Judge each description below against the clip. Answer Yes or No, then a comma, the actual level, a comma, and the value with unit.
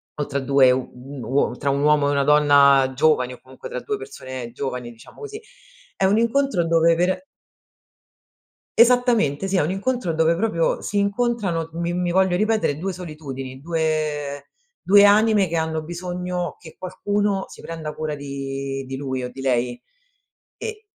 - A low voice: No, medium, 160 Hz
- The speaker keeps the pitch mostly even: No, wide, 5.7 semitones